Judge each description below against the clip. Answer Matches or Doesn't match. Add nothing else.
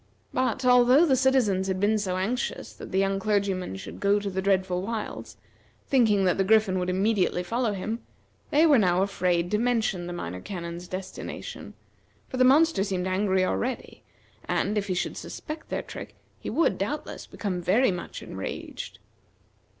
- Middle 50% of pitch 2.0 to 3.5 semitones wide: Doesn't match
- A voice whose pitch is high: Matches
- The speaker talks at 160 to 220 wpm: Matches